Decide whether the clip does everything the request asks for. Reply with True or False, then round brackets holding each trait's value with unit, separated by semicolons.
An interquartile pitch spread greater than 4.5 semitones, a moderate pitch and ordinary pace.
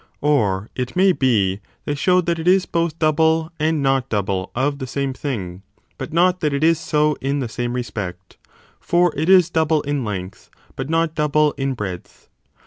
True (5.1 semitones; 145 Hz; 185 wpm)